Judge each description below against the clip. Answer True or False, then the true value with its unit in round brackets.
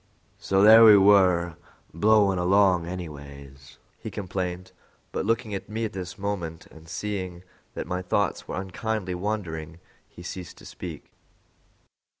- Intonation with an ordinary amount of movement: True (3.0 semitones)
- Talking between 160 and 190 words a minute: False (140 wpm)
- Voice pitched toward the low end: True (95 Hz)